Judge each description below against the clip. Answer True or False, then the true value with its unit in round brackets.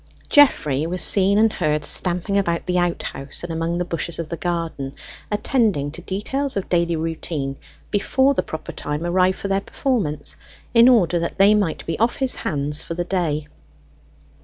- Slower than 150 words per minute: False (175 wpm)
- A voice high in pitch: False (175 Hz)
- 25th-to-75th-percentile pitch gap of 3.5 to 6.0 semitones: True (4.0 semitones)